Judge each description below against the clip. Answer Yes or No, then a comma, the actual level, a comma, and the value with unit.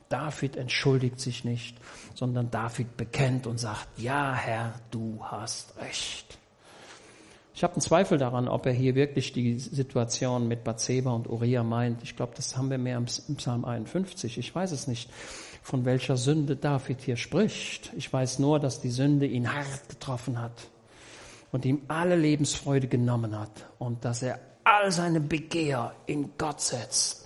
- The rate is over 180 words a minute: No, average, 165 wpm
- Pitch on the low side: Yes, low, 130 Hz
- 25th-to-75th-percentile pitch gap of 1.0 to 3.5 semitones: Yes, average, 3.2 semitones